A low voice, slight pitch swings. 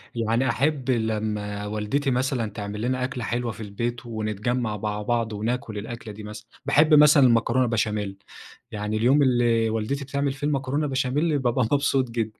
No: low, 120 Hz; average, 3.7 semitones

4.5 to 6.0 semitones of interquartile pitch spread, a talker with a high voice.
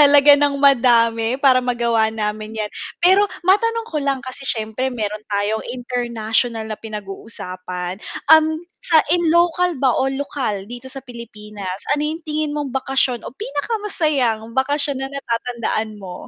Yes: average, 4.9 semitones; high, 245 Hz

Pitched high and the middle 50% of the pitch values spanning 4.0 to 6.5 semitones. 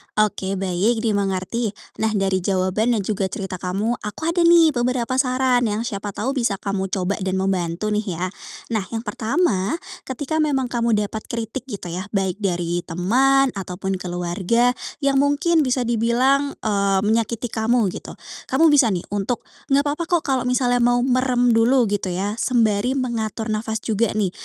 Yes: high, 220 Hz; average, 4.4 semitones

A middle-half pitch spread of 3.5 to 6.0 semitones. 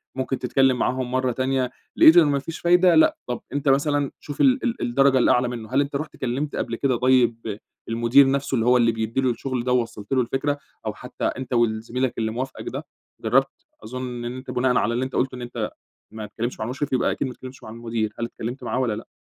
No: narrow, 2.4 semitones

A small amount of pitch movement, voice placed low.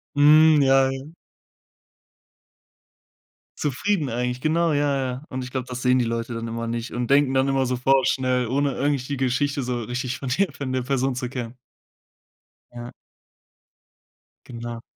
Yes: narrow, 2.1 semitones; low, 130 Hz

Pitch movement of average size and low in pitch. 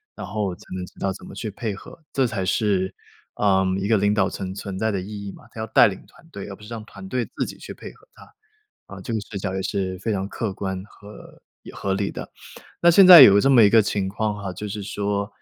No: narrow, 2.3 semitones; low, 100 Hz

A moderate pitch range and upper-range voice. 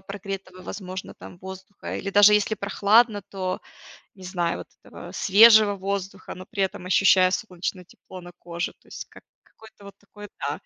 No: narrow, 1.8 semitones; high, 195 Hz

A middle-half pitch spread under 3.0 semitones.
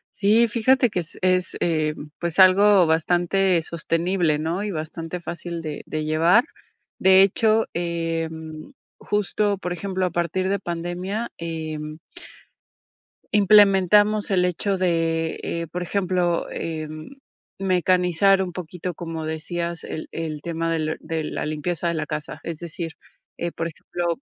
Yes: narrow, 2.6 semitones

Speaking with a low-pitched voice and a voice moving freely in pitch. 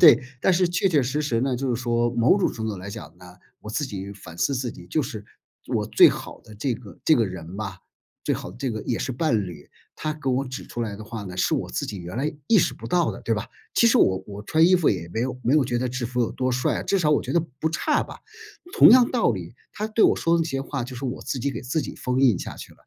Yes: low, 125 Hz; wide, 5.9 semitones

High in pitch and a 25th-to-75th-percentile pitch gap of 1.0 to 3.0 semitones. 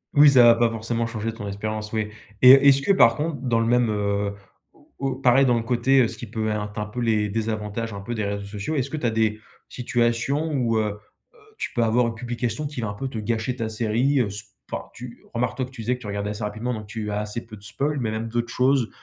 No: low, 115 Hz; average, 2.7 semitones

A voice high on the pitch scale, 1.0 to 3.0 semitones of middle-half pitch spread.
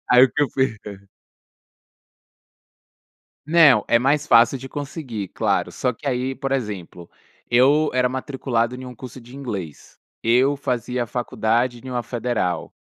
No: low, 125 Hz; narrow, 2.4 semitones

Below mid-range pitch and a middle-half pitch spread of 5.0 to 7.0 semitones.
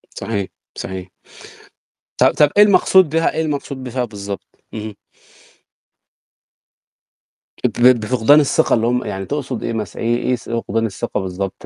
Yes: low, 115 Hz; average, 5.3 semitones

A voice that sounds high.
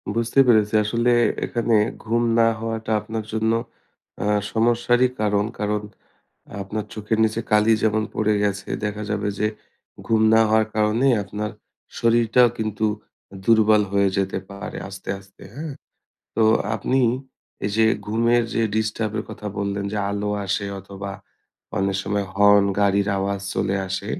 No: low, 105 Hz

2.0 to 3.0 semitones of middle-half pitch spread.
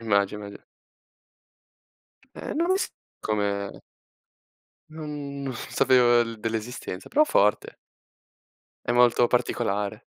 No: average, 4.6 semitones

